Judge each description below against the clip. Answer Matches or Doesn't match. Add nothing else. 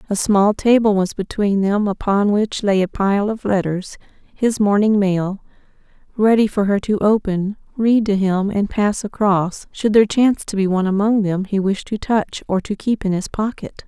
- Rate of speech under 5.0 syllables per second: Matches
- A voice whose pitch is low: Doesn't match